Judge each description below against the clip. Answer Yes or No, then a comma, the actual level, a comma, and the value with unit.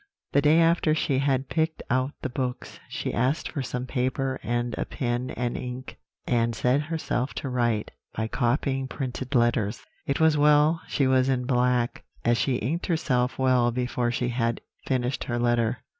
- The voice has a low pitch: Yes, low, 125 Hz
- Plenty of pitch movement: No, narrow, 2.4 semitones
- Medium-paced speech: Yes, average, 175 wpm